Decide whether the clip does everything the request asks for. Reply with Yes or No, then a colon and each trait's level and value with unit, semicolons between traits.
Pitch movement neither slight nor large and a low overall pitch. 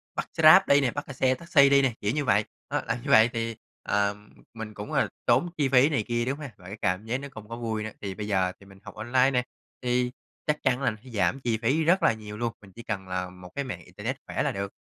Yes: average, 4.5 semitones; low, 115 Hz